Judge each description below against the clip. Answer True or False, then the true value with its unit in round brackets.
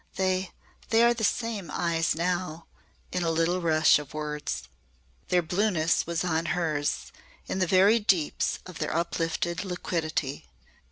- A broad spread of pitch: False (2.6 semitones)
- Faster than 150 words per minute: False (145 wpm)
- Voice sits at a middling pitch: True (170 Hz)